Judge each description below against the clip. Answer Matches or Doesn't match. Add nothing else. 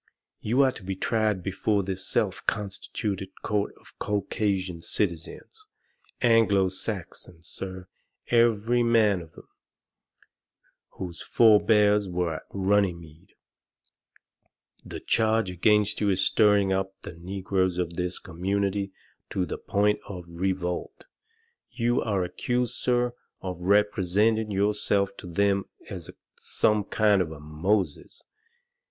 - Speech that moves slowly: Matches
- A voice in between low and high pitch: Doesn't match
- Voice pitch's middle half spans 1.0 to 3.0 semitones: Matches